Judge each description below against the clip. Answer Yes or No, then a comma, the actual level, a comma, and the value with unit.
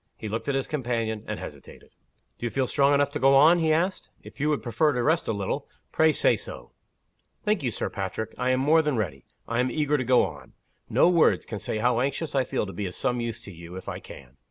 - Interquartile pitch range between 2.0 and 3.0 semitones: No, average, 5.1 semitones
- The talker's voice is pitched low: Yes, low, 130 Hz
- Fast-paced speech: Yes, fast, 250 wpm